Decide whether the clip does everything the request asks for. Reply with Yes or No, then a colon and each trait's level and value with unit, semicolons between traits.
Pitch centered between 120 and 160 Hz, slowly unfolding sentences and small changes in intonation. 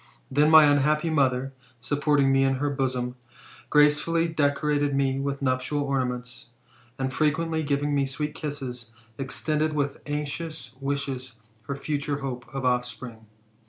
Yes: medium, 140 Hz; slow, 130 wpm; narrow, 2.2 semitones